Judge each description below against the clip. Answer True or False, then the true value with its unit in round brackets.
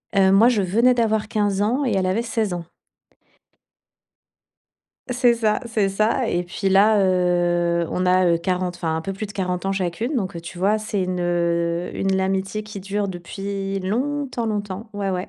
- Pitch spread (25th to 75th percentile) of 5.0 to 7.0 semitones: False (2.9 semitones)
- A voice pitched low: False (195 Hz)